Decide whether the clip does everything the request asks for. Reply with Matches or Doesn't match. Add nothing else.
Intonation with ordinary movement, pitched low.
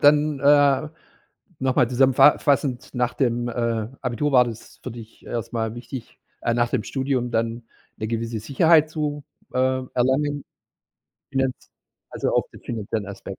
Matches